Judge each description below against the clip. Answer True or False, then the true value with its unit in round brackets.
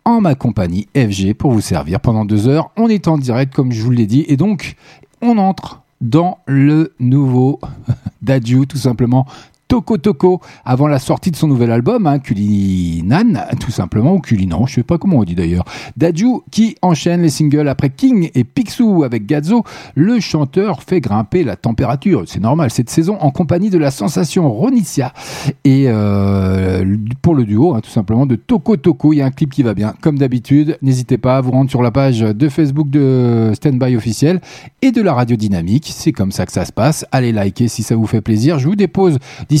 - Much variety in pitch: True (5.8 semitones)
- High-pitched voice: False (135 Hz)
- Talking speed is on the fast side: False (205 wpm)